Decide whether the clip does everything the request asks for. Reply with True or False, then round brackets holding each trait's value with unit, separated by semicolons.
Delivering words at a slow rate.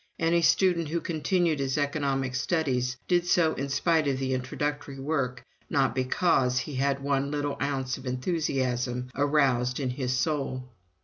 False (160 wpm)